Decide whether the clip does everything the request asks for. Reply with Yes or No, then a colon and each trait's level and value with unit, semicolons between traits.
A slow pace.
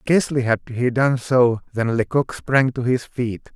No: average, 185 wpm